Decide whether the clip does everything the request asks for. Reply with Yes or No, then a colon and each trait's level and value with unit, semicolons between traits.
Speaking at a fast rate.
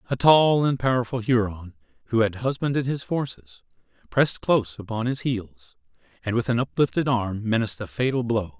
No: average, 170 wpm